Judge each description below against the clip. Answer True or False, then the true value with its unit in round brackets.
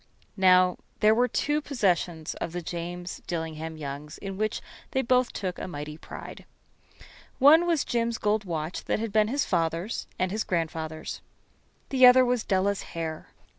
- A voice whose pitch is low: False (185 Hz)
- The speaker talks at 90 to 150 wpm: False (160 wpm)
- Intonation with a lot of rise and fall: True (6.1 semitones)